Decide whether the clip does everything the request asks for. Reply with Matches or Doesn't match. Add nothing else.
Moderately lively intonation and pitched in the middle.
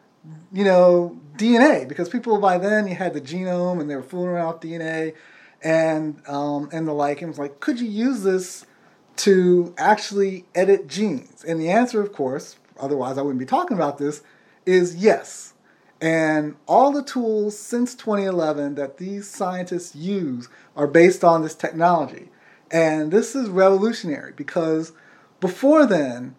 Matches